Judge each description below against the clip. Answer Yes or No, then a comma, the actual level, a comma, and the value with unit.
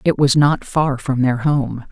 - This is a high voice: No, low, 135 Hz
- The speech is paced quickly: Yes, fast, 220 wpm